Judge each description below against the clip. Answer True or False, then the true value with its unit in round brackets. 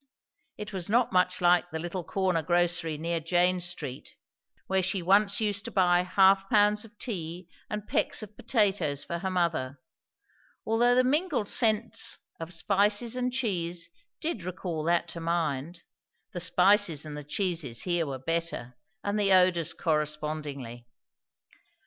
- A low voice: False (180 Hz)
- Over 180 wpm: False (150 wpm)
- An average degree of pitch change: True (3.7 semitones)